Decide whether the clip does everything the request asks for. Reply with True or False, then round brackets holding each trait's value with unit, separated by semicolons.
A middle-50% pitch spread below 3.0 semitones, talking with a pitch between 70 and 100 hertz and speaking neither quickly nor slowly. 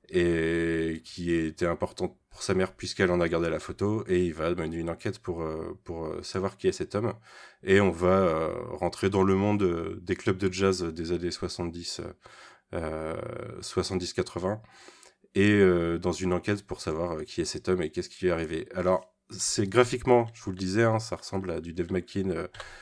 True (2.4 semitones; 90 Hz; 195 wpm)